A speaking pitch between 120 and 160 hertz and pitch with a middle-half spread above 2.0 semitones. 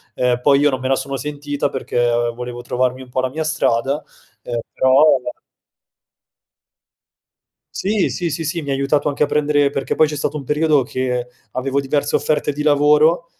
Yes: medium, 140 Hz; narrow, 2.6 semitones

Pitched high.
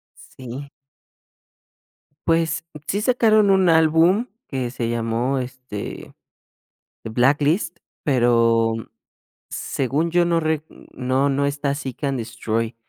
No: medium, 140 Hz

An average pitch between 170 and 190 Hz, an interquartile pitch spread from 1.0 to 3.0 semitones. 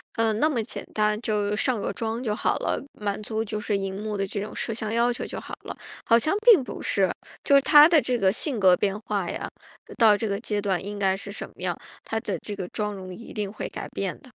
No: high, 210 Hz; narrow, 2.4 semitones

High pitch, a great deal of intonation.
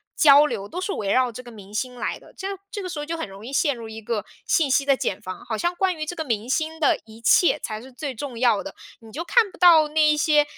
Yes: very high, 275 Hz; wide, 6.0 semitones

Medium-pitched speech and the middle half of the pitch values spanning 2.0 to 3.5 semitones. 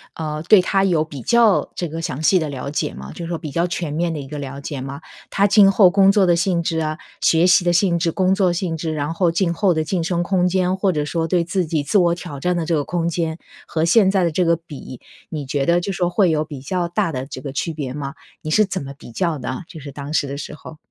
Yes: medium, 165 Hz; average, 3.2 semitones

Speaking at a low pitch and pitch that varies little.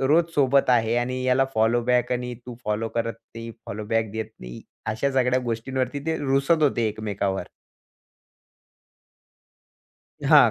No: low, 120 Hz; average, 3.0 semitones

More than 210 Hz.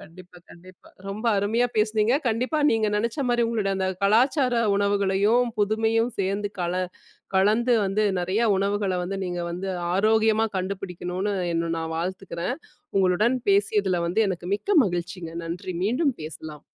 No: high, 200 Hz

